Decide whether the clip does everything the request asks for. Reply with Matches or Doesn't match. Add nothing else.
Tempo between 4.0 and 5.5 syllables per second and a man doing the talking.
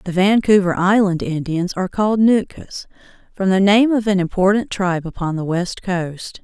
Doesn't match